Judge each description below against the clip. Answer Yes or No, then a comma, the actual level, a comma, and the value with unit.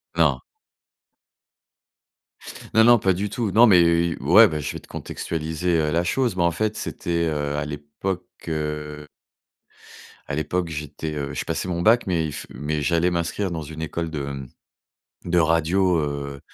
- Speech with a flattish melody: No, average, 3.1 semitones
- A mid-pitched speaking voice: No, very low, 80 Hz